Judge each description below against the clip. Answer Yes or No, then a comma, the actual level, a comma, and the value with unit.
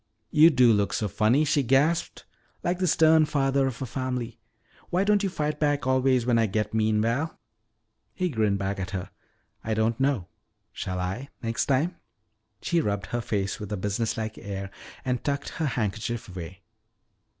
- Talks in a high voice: No, low, 120 Hz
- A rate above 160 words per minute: Yes, average, 170 wpm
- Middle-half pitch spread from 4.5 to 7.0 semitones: Yes, average, 5.3 semitones